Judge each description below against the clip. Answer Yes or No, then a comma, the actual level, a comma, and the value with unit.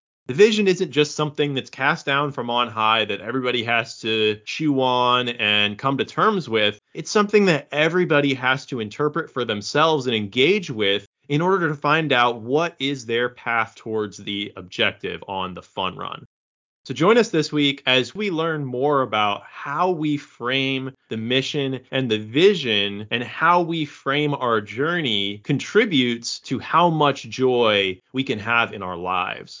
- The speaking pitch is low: Yes, low, 130 Hz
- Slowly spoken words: No, average, 170 wpm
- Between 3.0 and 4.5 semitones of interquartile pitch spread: No, average, 5.0 semitones